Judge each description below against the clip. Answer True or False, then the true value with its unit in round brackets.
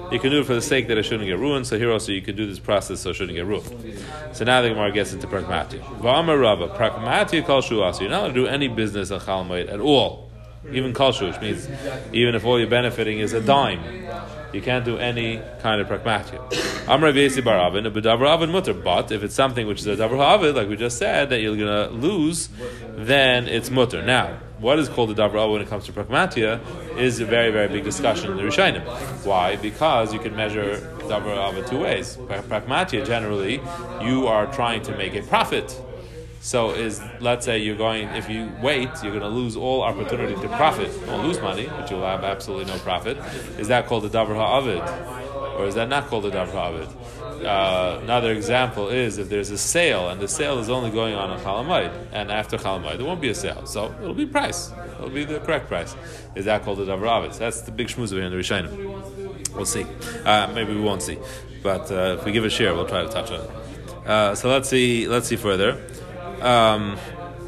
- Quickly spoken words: True (210 wpm)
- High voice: False (115 Hz)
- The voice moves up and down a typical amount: True (3.5 semitones)